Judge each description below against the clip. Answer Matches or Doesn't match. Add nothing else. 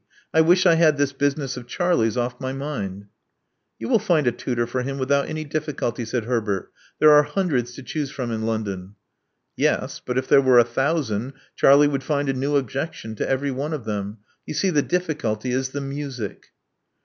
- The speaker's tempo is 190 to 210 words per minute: Matches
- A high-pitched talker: Doesn't match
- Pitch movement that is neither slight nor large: Matches